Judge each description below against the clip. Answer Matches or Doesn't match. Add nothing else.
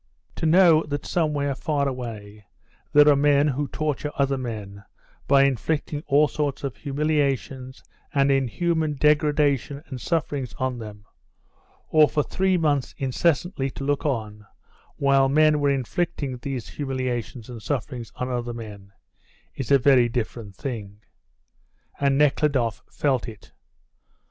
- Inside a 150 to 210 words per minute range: Doesn't match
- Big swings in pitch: Doesn't match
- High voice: Doesn't match